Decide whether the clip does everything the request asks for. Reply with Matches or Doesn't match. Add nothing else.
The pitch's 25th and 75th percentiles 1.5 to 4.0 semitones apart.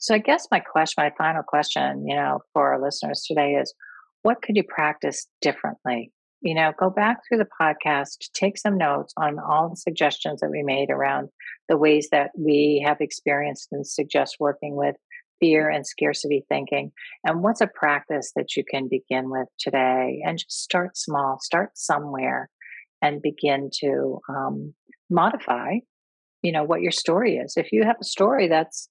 Matches